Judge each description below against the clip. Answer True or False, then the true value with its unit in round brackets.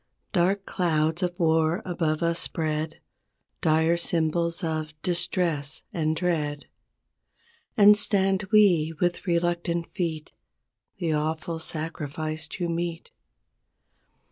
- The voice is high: False (165 Hz)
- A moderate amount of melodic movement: False (1.9 semitones)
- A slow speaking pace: True (100 wpm)